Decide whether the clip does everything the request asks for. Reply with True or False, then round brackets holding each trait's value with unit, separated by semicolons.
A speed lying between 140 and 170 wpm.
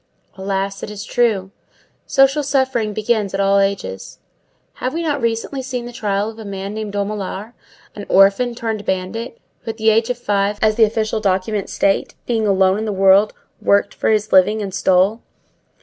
False (180 wpm)